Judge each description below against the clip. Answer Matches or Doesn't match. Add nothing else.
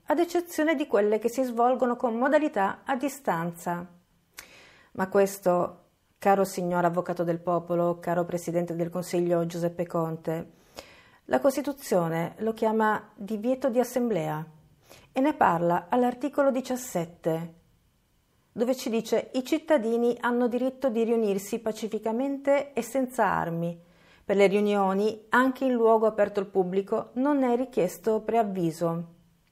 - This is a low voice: Doesn't match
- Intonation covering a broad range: Matches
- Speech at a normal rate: Matches